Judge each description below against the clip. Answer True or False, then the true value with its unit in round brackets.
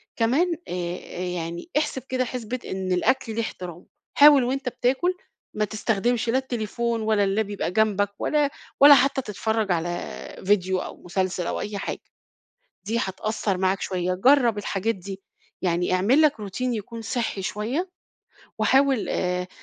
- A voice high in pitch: True (215 Hz)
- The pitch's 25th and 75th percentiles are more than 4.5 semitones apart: True (5.1 semitones)